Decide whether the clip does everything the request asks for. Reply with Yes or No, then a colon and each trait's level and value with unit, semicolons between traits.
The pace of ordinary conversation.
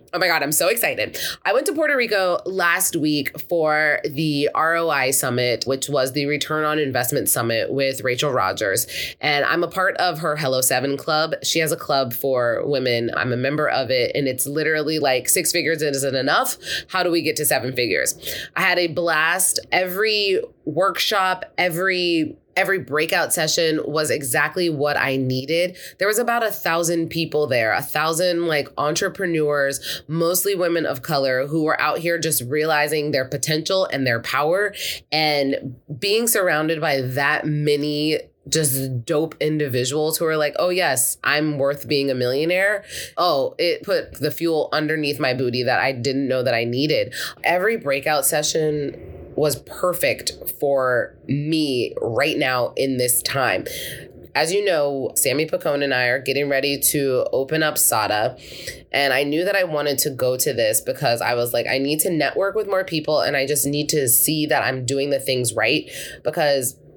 Yes: average, 175 wpm